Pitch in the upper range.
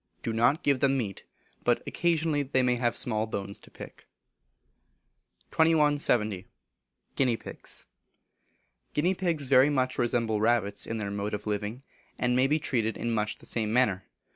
No: low, 120 Hz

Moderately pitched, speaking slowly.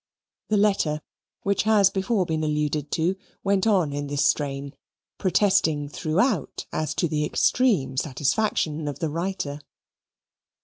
Yes: medium, 160 Hz; slow, 130 wpm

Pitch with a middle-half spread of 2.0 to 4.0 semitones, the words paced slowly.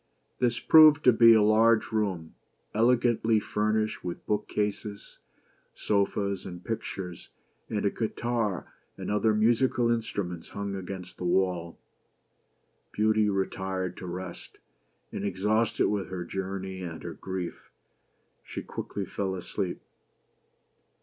Yes: average, 2.8 semitones; slow, 125 wpm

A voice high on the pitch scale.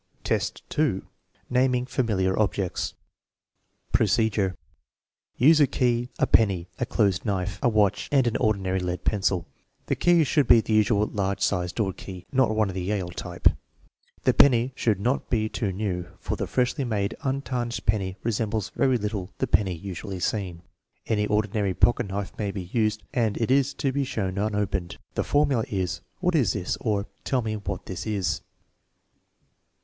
No: low, 105 Hz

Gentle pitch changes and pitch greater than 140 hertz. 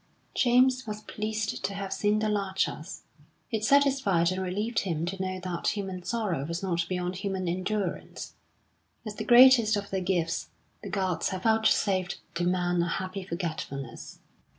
No: average, 3.1 semitones; high, 190 Hz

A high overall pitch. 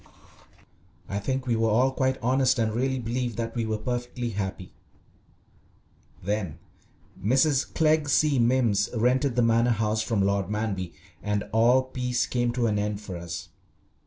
No: low, 115 Hz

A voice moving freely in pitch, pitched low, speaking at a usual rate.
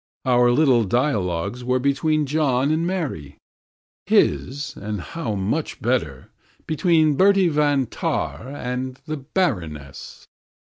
No: wide, 5.9 semitones; low, 130 Hz; slow, 110 wpm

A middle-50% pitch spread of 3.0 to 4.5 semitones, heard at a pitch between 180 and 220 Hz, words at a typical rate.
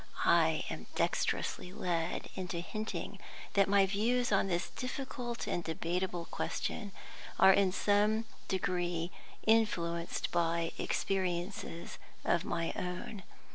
No: average, 3.3 semitones; medium, 185 Hz; slow, 110 wpm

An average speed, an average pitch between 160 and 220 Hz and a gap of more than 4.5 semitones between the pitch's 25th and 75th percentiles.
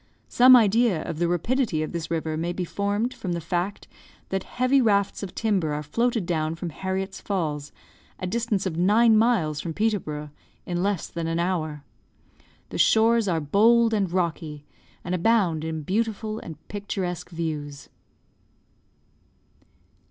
Yes: average, 150 wpm; medium, 185 Hz; average, 5.1 semitones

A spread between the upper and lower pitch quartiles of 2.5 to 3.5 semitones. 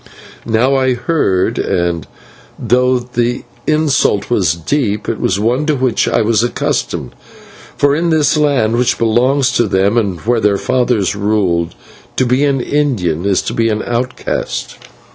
No: average, 4.3 semitones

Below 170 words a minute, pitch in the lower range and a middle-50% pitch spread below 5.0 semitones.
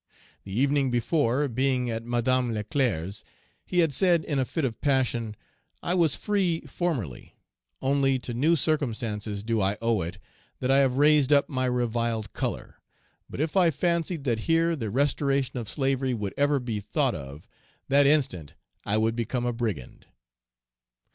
Yes: average, 160 wpm; low, 130 Hz; average, 4.3 semitones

